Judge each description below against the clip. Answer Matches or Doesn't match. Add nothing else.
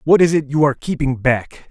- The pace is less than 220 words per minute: Doesn't match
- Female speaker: Doesn't match